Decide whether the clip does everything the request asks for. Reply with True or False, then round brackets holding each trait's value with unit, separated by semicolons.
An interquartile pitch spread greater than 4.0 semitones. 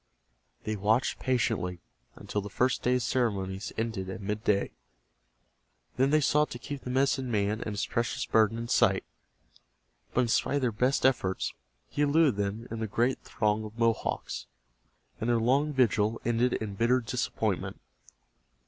False (3.3 semitones)